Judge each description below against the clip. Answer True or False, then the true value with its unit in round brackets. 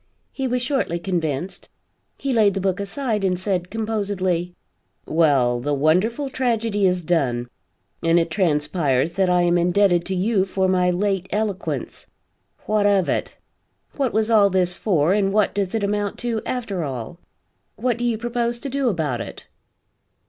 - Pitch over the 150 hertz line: True (190 Hz)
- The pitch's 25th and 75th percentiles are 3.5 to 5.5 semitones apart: True (4.2 semitones)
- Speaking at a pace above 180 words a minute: False (165 wpm)